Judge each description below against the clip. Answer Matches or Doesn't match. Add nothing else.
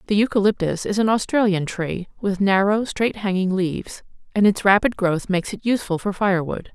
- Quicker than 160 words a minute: Matches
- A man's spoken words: Doesn't match